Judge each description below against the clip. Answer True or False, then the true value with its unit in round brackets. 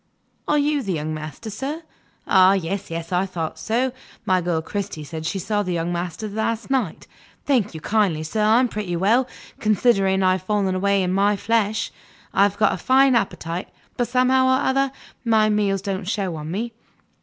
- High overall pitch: True (200 Hz)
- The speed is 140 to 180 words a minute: False (190 wpm)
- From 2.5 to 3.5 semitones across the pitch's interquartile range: False (4.2 semitones)